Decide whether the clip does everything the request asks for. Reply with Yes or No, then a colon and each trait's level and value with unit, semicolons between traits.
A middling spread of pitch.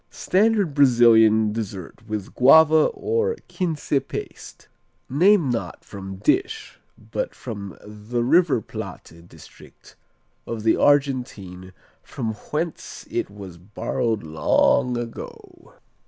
No: wide, 7.0 semitones